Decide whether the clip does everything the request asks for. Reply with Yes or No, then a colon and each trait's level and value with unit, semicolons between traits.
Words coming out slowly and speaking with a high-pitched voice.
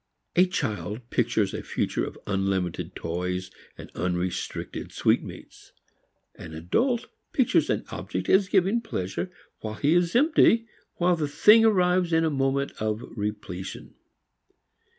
No: slow, 130 wpm; low, 135 Hz